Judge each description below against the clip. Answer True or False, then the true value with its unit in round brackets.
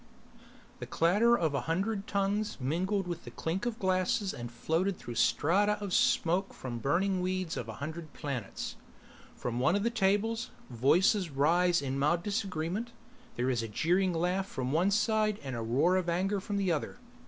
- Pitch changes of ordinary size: False (5.8 semitones)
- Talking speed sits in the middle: True (180 wpm)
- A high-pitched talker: False (180 Hz)